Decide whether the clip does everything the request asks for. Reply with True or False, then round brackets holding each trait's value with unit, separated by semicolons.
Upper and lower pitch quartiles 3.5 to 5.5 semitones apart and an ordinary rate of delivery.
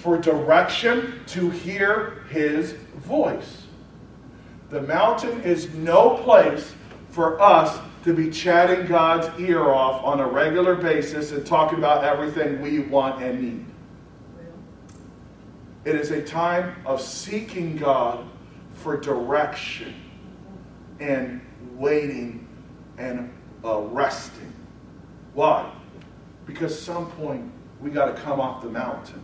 False (3.8 semitones; 115 wpm)